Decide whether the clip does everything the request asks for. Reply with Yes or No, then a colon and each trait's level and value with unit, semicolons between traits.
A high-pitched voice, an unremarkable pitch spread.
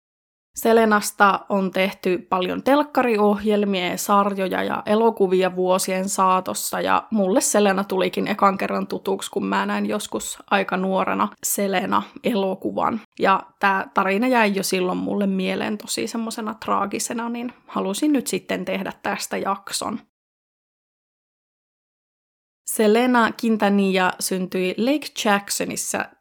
Yes: high, 200 Hz; average, 3.0 semitones